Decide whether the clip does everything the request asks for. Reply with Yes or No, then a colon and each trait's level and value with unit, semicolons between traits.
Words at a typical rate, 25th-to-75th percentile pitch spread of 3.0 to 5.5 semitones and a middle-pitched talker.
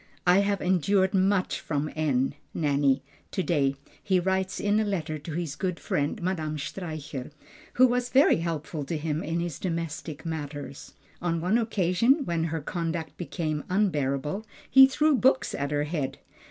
Yes: average, 160 wpm; average, 4.2 semitones; medium, 170 Hz